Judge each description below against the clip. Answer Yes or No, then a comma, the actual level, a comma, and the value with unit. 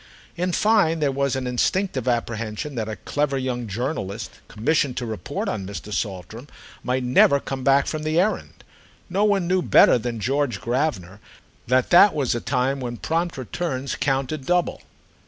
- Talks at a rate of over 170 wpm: No, average, 165 wpm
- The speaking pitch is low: Yes, low, 130 Hz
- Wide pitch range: No, average, 4.8 semitones